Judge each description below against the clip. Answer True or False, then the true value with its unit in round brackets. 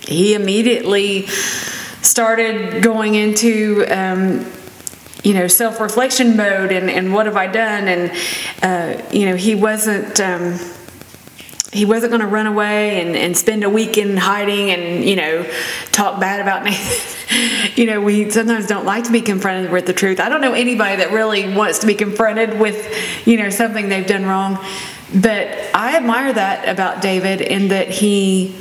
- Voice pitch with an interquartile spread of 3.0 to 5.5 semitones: False (2.4 semitones)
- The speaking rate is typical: True (170 wpm)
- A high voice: True (205 Hz)